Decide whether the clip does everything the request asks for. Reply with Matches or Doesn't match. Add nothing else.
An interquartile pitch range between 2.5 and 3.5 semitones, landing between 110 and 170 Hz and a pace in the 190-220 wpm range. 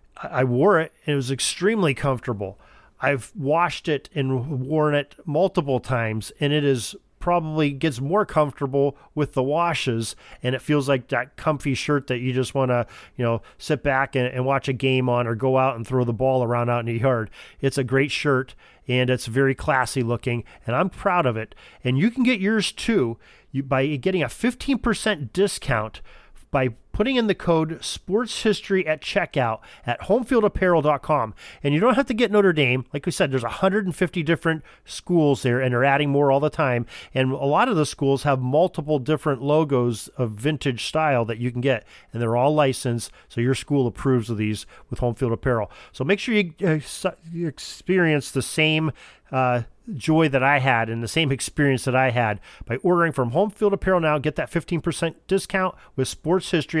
Doesn't match